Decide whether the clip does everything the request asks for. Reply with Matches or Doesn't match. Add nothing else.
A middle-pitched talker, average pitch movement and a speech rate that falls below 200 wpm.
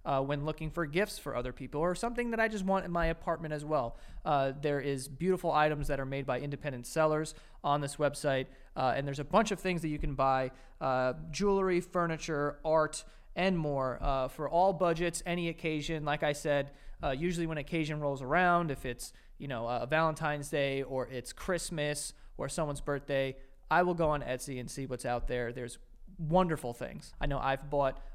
Doesn't match